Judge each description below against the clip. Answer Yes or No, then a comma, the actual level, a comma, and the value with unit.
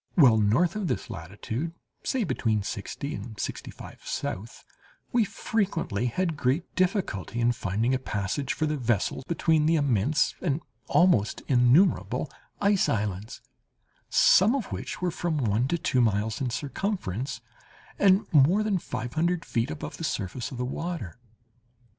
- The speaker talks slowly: No, average, 150 wpm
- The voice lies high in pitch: No, low, 135 Hz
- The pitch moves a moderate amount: No, wide, 7.5 semitones